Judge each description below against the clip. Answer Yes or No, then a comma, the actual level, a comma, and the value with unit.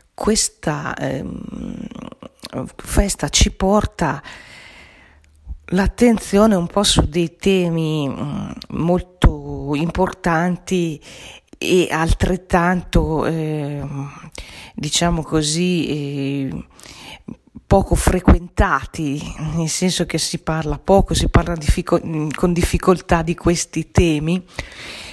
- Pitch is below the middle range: No, medium, 170 Hz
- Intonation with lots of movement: No, average, 3.5 semitones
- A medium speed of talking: No, slow, 85 wpm